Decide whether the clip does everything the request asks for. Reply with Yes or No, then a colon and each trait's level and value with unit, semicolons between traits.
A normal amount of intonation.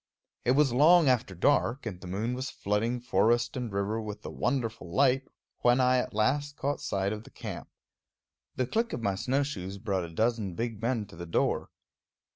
Yes: average, 4.3 semitones